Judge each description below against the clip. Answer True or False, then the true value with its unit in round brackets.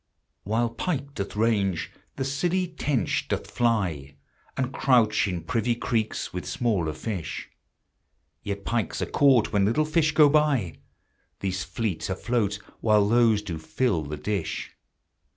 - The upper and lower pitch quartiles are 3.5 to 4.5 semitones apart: False (5.2 semitones)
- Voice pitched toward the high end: False (110 Hz)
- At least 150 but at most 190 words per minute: False (135 wpm)